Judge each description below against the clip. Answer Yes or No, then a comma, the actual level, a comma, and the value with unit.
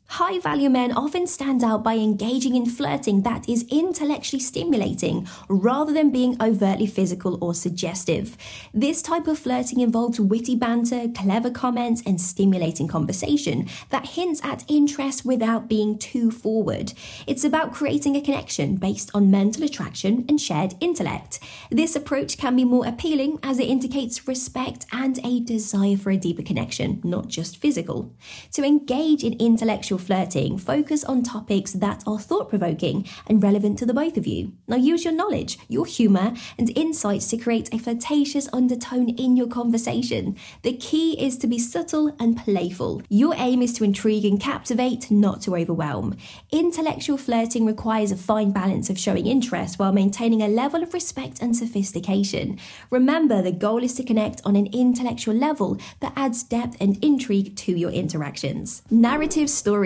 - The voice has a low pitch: No, high, 235 Hz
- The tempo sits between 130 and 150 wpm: No, average, 160 wpm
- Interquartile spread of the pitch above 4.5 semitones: Yes, average, 5.1 semitones